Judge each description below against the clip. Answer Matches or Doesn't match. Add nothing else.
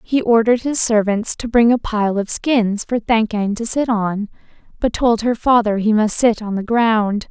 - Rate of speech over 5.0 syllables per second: Doesn't match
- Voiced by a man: Doesn't match